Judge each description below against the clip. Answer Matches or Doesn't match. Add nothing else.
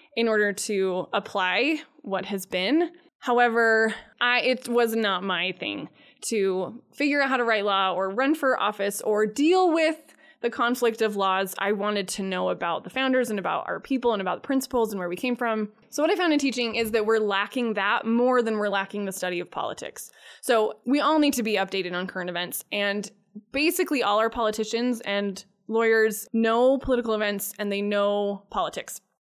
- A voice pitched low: Doesn't match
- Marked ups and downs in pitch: Doesn't match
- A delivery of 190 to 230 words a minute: Matches